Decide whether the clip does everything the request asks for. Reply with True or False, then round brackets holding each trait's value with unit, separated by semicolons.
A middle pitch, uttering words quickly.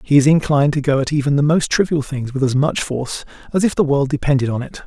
True (145 Hz; 270 wpm)